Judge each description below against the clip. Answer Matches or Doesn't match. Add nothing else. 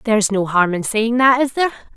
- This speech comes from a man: Doesn't match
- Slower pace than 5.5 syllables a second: Doesn't match